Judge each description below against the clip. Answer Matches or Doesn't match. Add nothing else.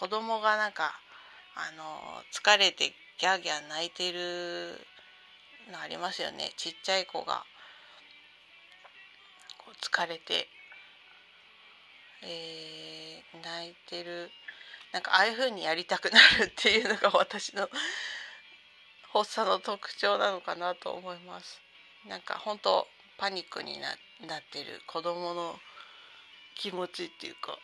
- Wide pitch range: Doesn't match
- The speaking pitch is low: Doesn't match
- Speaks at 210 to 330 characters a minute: Matches